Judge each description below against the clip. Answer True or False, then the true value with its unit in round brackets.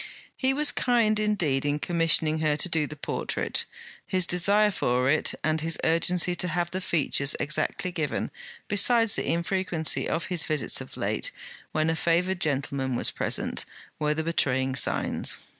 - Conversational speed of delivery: True (160 wpm)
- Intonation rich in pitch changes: False (3.6 semitones)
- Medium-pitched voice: True (165 Hz)